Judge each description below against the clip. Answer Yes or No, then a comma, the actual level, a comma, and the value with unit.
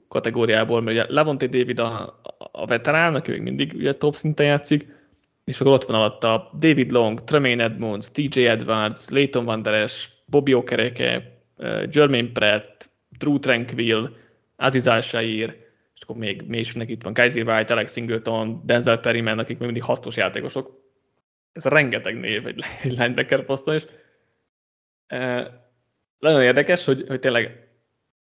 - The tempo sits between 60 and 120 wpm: No, average, 140 wpm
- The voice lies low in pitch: Yes, low, 120 Hz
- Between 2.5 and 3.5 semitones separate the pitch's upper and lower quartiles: Yes, average, 3.1 semitones